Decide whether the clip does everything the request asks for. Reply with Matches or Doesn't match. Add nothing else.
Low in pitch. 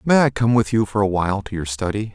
Matches